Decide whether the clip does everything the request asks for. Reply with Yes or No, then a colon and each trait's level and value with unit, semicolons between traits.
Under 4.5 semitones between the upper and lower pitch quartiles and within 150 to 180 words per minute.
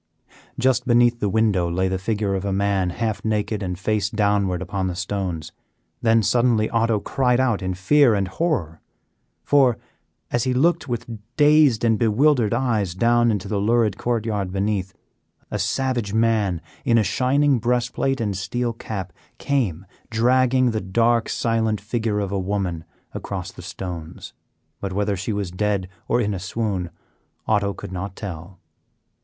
Yes: average, 3.7 semitones; average, 160 wpm